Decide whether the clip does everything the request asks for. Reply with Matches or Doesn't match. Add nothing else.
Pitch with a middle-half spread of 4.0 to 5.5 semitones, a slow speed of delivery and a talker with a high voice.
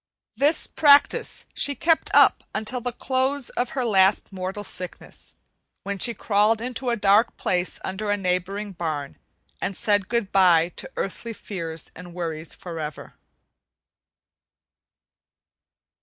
Matches